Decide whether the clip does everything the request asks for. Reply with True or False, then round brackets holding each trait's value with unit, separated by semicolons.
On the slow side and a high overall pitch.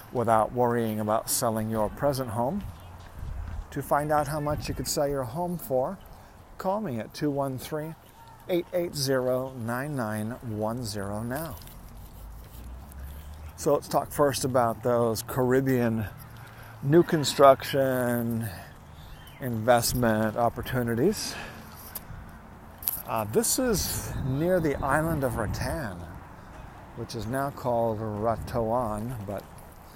False (95 wpm; 120 Hz)